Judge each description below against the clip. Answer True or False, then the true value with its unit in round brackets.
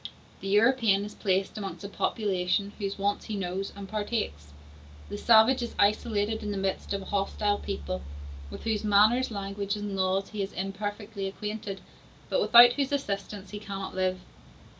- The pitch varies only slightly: True (1.6 semitones)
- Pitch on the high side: True (205 Hz)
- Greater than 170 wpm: False (165 wpm)